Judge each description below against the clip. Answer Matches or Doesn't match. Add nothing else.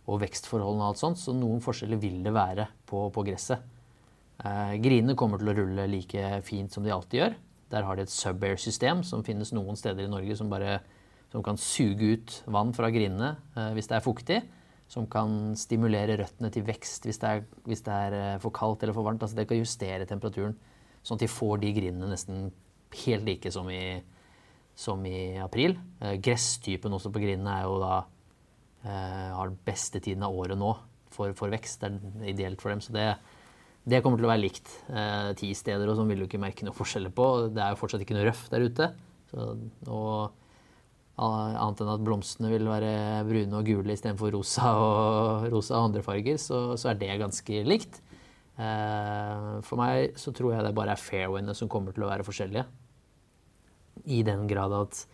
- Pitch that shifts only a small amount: Matches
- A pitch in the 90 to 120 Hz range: Matches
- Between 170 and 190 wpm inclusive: Doesn't match